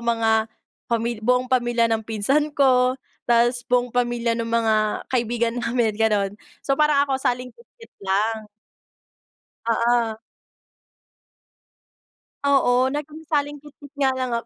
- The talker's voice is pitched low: No, high, 240 Hz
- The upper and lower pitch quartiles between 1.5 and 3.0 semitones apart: Yes, narrow, 2.6 semitones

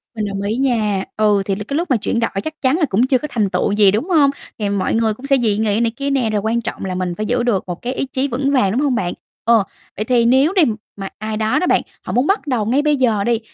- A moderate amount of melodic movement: Yes, average, 4.5 semitones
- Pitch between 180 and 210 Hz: No, high, 230 Hz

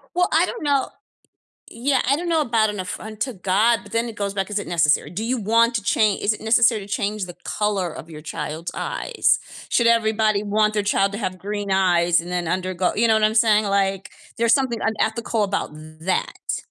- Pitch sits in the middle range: No, high, 210 Hz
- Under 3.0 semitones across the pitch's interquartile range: No, average, 3.5 semitones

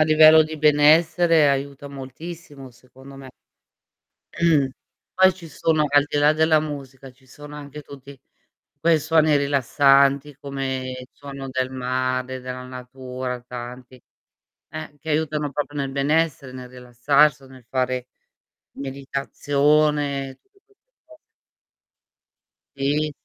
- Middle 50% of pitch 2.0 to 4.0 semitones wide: Yes, narrow, 2.6 semitones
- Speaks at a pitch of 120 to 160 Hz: Yes, medium, 140 Hz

